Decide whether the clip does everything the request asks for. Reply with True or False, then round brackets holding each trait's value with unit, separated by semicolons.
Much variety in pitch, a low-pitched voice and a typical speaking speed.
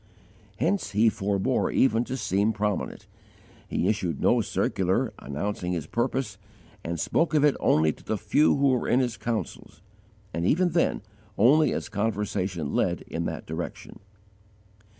True (5.7 semitones; 110 Hz; 150 wpm)